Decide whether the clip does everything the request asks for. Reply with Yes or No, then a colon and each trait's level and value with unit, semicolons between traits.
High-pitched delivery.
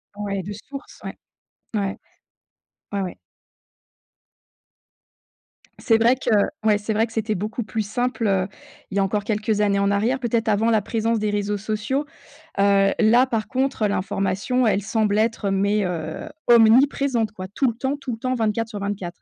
Yes: high, 215 Hz